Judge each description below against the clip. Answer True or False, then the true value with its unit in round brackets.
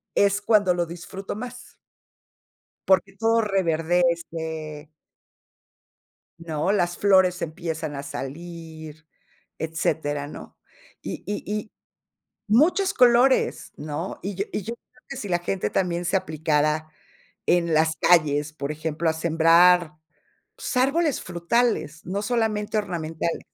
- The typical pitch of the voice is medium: True (175 Hz)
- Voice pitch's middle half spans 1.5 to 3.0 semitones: False (4.4 semitones)